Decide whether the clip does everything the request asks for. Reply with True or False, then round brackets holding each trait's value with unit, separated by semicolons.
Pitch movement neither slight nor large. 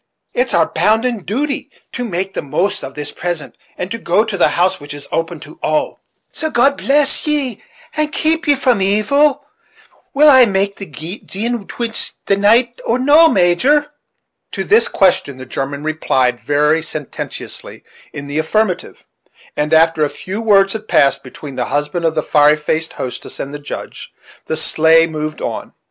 False (7.8 semitones)